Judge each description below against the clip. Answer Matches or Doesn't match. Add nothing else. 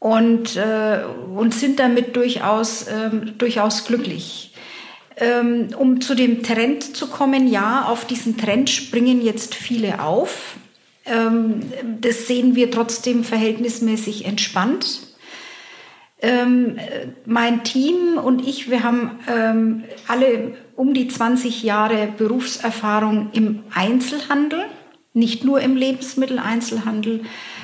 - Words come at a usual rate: Doesn't match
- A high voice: Matches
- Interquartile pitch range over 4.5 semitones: Doesn't match